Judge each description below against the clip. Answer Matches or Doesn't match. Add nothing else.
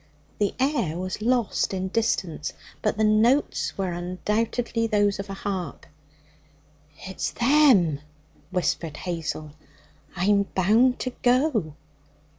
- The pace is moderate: Doesn't match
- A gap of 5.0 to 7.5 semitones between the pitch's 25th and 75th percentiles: Doesn't match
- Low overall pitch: Doesn't match